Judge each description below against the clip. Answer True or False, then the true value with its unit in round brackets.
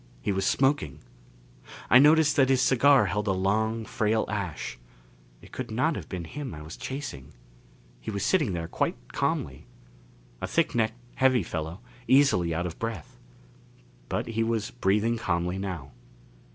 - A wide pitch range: True (6.4 semitones)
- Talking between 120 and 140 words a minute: False (155 wpm)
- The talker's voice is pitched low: True (110 Hz)